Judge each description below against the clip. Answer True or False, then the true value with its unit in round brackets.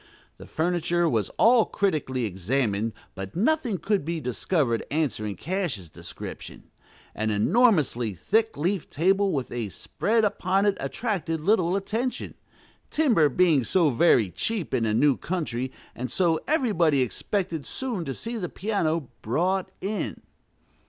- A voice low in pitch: False (165 Hz)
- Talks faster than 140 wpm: False (135 wpm)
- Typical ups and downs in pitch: False (7.9 semitones)